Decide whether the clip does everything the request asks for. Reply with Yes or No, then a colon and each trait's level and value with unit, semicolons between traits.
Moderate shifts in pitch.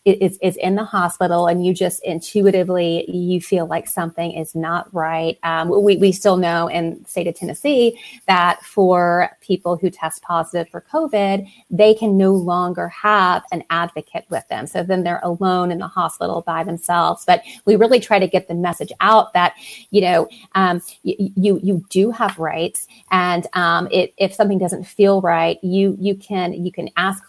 No: narrow, 2.3 semitones